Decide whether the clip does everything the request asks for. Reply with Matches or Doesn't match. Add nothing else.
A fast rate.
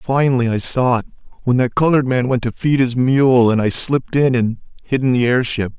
Matches